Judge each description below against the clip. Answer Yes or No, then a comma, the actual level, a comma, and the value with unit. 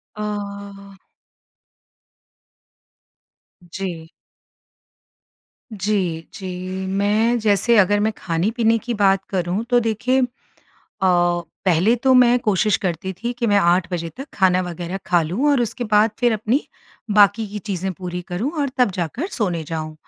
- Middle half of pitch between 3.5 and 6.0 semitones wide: Yes, average, 3.8 semitones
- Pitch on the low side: No, high, 200 Hz